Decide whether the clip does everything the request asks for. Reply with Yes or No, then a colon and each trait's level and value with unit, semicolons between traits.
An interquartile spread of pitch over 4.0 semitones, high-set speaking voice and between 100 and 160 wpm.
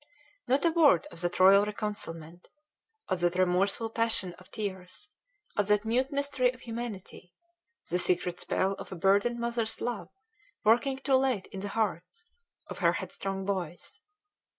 Yes: average, 4.5 semitones; high, 205 Hz; average, 150 wpm